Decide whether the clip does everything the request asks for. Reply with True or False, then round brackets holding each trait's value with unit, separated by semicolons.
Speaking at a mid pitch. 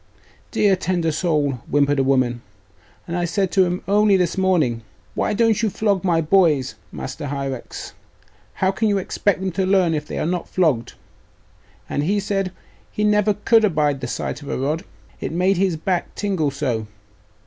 True (175 Hz)